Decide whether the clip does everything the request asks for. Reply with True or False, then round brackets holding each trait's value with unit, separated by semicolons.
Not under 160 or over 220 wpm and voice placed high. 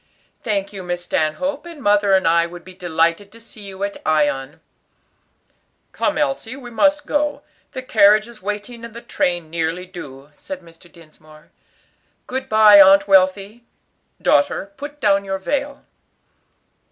False (150 wpm; 200 Hz)